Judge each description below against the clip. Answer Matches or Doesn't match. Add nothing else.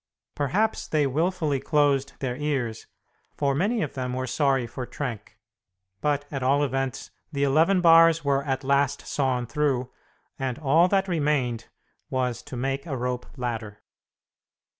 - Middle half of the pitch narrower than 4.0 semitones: Matches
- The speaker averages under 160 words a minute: Matches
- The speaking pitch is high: Doesn't match